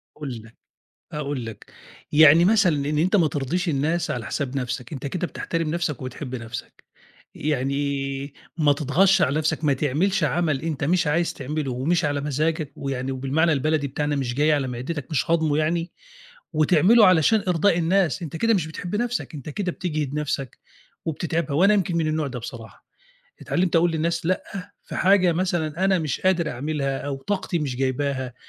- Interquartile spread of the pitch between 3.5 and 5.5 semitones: Yes, average, 3.8 semitones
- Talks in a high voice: No, medium, 155 Hz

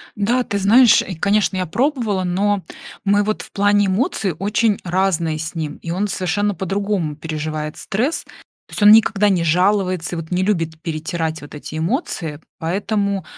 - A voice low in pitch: No, high, 190 Hz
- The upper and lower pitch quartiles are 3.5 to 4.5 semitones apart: Yes, average, 3.9 semitones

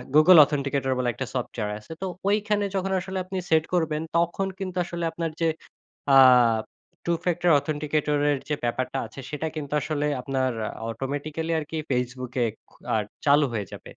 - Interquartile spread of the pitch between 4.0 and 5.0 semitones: Yes, average, 4.3 semitones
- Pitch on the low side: No, medium, 150 Hz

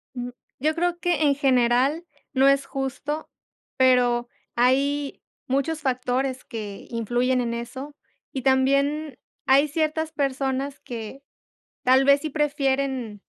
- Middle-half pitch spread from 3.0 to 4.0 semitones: No, narrow, 2.4 semitones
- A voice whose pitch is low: No, very high, 270 Hz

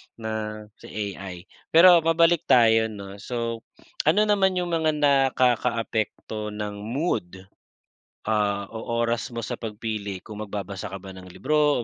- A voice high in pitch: No, low, 115 Hz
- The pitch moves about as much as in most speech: No, wide, 6.4 semitones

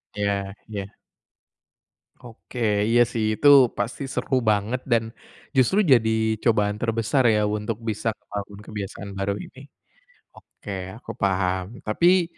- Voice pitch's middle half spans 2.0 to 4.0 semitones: Yes, narrow, 2.6 semitones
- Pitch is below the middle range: Yes, low, 110 Hz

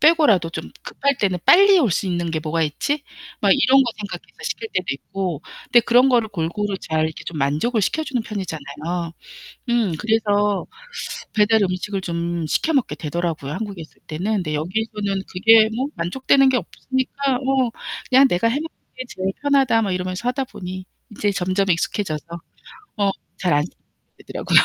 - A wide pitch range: Yes, wide, 6.1 semitones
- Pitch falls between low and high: No, high, 200 Hz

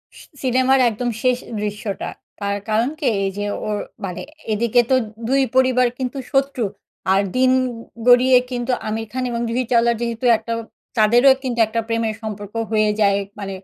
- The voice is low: No, high, 235 Hz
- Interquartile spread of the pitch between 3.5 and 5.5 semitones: No, average, 3.0 semitones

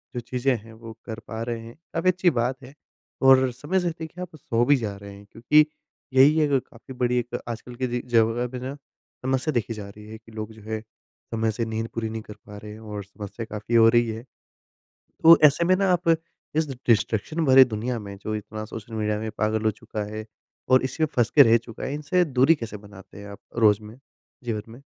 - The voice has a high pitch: No, low, 115 Hz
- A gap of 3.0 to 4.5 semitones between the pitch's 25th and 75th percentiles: Yes, average, 3.4 semitones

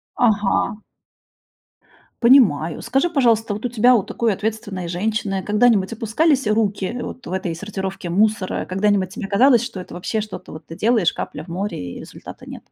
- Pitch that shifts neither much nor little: Yes, average, 3.6 semitones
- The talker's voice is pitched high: Yes, high, 210 Hz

